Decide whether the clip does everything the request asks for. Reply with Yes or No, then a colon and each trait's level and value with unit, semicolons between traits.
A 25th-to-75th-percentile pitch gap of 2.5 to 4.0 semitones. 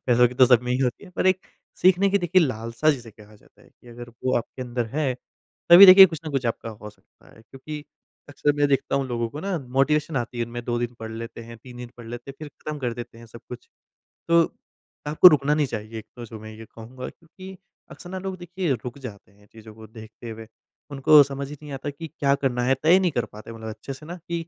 No: average, 4.7 semitones